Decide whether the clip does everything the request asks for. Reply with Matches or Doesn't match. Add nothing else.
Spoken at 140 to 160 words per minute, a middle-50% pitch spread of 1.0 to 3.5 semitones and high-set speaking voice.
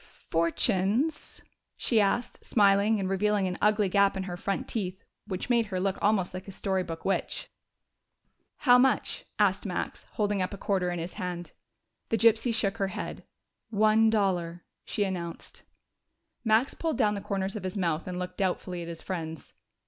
Doesn't match